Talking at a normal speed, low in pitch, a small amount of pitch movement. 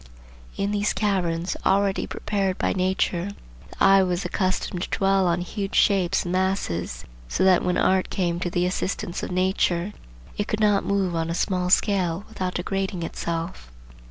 No: average, 165 wpm; medium, 185 Hz; narrow, 1.9 semitones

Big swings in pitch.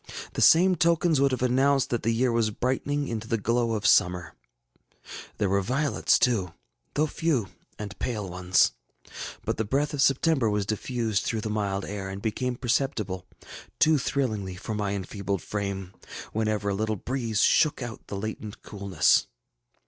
No: average, 4.6 semitones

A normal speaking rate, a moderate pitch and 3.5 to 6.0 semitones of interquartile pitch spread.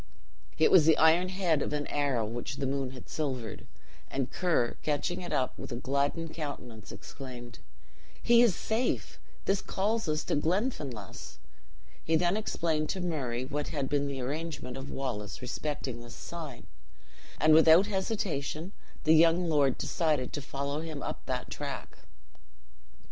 Yes: average, 155 wpm; medium, 150 Hz; average, 4.0 semitones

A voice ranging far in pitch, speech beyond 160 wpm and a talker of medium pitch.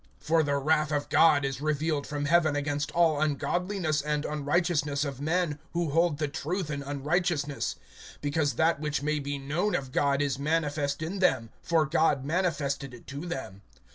No: narrow, 2.4 semitones; average, 170 wpm; medium, 150 Hz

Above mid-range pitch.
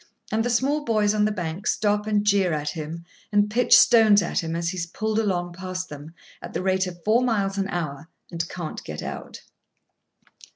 Yes: high, 195 Hz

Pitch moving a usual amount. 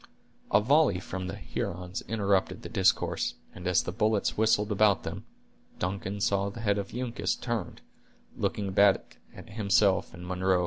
No: narrow, 2.3 semitones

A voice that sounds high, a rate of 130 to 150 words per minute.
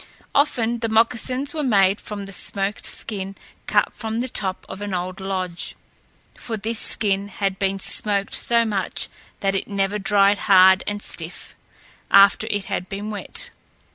No: high, 200 Hz; average, 160 wpm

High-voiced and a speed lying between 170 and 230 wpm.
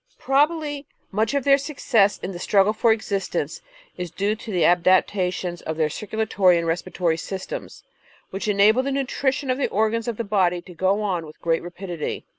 Yes: high, 200 Hz; average, 180 wpm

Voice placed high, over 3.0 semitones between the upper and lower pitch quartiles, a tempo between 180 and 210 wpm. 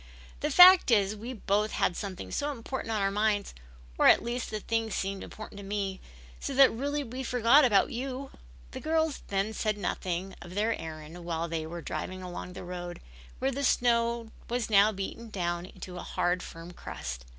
Yes: high, 210 Hz; average, 4.7 semitones; average, 190 wpm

